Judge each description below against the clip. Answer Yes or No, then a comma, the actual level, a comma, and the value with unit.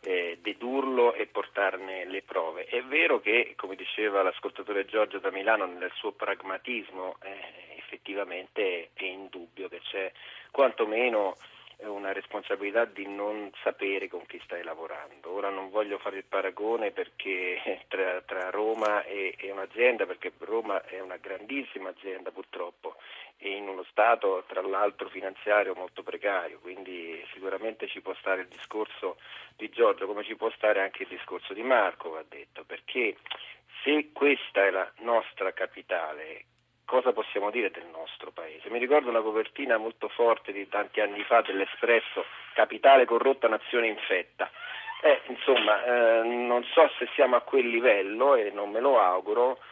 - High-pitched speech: No, low, 135 Hz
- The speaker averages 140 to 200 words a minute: Yes, average, 150 wpm